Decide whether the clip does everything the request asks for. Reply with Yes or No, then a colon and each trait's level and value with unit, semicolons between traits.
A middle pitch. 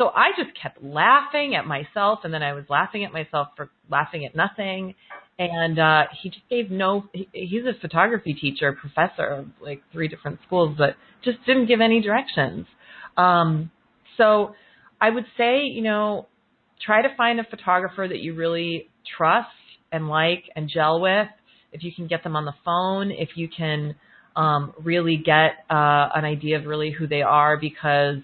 Yes: medium, 165 Hz